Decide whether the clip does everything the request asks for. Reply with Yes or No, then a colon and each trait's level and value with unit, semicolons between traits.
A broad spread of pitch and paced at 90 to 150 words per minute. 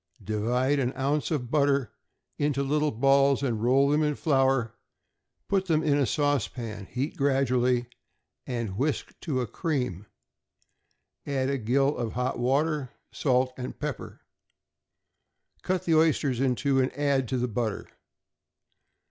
No: average, 2.7 semitones; average, 140 wpm